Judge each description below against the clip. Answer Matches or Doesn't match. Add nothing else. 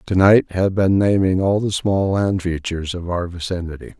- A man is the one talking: Matches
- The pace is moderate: Matches